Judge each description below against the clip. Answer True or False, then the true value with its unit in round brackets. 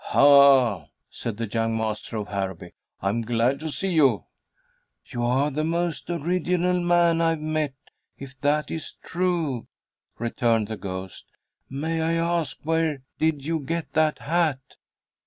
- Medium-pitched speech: True (145 Hz)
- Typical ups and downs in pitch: False (5.8 semitones)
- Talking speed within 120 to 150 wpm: True (140 wpm)